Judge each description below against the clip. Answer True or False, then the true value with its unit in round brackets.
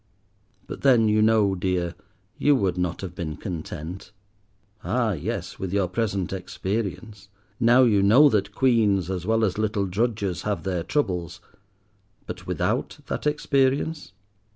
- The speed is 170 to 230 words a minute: False (135 wpm)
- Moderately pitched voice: False (100 Hz)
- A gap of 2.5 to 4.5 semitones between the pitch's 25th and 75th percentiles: True (3.7 semitones)